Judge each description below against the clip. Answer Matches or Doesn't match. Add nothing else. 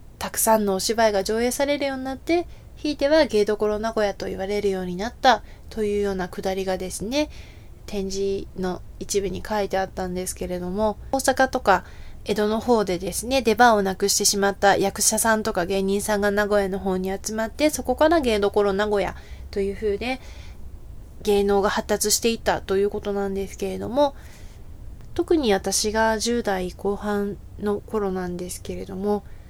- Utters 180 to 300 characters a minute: Doesn't match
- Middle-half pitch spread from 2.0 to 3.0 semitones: Matches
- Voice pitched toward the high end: Matches